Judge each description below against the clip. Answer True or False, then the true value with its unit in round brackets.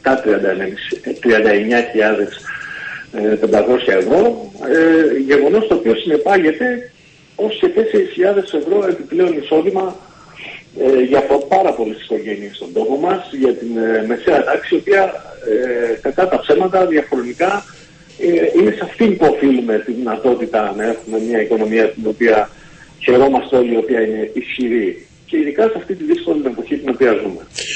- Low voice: False (145 Hz)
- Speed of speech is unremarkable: True (130 wpm)